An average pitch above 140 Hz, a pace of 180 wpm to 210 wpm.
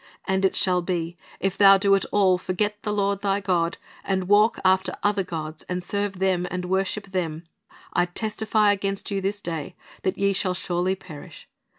Yes: high, 190 Hz; average, 185 wpm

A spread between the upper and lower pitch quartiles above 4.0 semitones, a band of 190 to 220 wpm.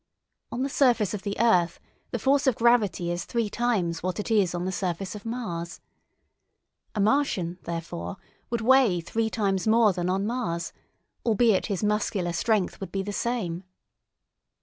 No: average, 4.8 semitones; average, 165 wpm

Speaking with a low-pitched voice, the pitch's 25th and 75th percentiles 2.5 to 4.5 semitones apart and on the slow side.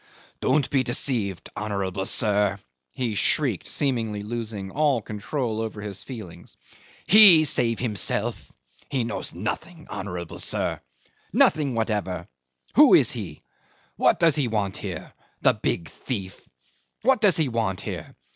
No: low, 110 Hz; average, 5.2 semitones; slow, 130 wpm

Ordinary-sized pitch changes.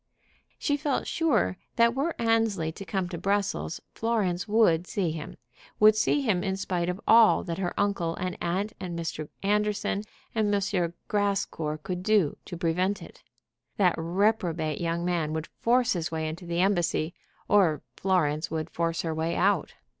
Yes: average, 3.8 semitones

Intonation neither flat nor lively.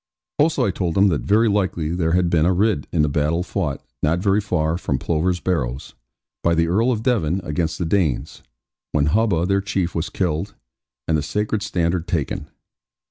Yes: average, 3.8 semitones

